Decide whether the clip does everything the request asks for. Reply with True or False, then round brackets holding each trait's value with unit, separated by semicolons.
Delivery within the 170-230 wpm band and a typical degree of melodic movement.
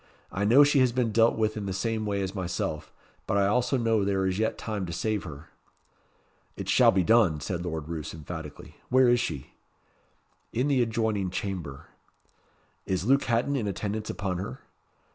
True (180 wpm; 4.1 semitones)